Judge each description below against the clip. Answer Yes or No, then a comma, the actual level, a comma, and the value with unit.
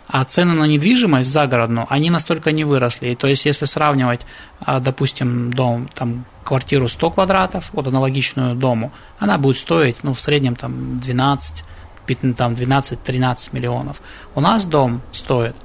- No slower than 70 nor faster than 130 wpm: No, average, 140 wpm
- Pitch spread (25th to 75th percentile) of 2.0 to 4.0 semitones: Yes, average, 3.3 semitones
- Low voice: Yes, low, 130 Hz